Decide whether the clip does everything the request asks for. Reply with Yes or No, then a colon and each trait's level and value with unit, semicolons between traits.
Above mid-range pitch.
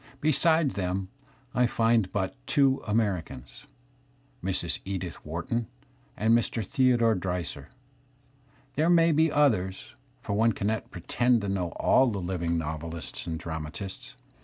No: low, 100 Hz